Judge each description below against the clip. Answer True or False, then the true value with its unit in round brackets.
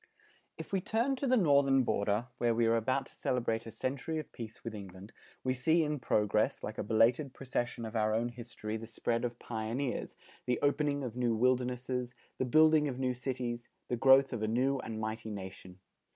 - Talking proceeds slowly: False (195 wpm)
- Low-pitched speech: True (120 Hz)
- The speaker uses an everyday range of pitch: True (3.2 semitones)